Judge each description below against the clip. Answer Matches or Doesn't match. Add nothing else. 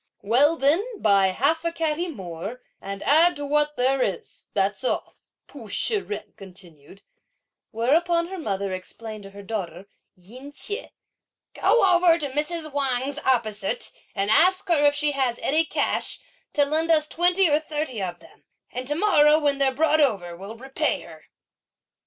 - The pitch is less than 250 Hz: Doesn't match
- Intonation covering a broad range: Matches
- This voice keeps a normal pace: Matches